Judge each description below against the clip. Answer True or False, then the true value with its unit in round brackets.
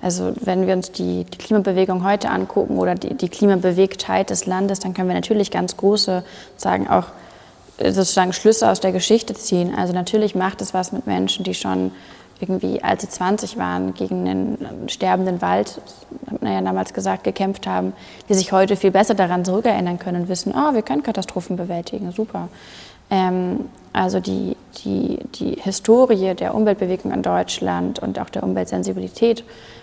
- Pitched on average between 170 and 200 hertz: True (185 Hz)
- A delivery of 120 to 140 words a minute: False (165 wpm)